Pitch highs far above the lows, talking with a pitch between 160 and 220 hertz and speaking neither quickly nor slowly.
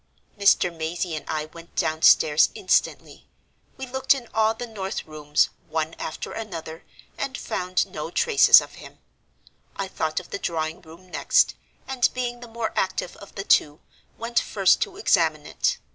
Yes: wide, 6.8 semitones; medium, 185 Hz; average, 160 wpm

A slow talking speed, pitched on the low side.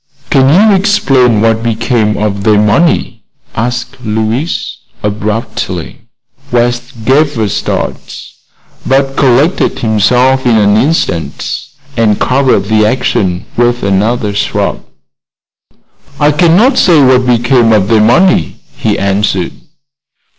Yes: slow, 110 wpm; low, 120 Hz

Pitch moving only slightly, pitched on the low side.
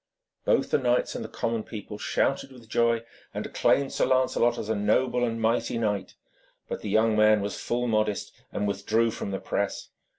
Yes: narrow, 2.1 semitones; low, 115 Hz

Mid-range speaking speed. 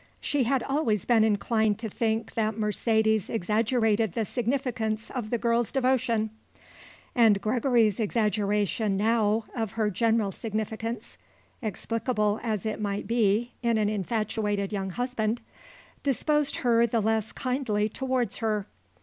No: slow, 130 wpm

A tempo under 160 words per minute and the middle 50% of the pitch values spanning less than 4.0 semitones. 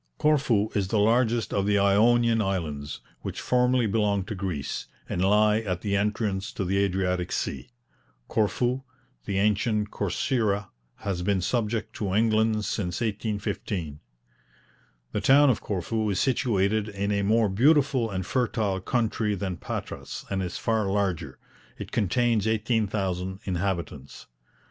Yes: slow, 135 wpm; average, 2.8 semitones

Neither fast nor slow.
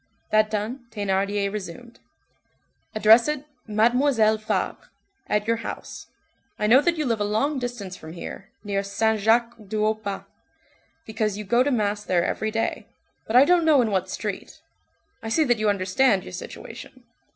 Yes: average, 170 wpm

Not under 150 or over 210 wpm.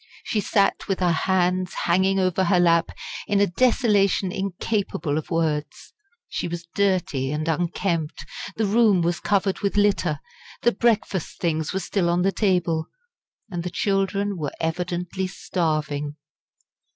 No: average, 140 wpm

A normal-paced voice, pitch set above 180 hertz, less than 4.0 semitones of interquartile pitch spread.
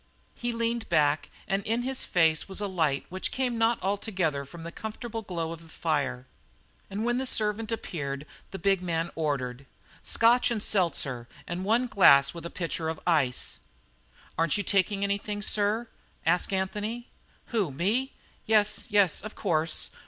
No: average, 160 wpm; high, 190 Hz; average, 5.3 semitones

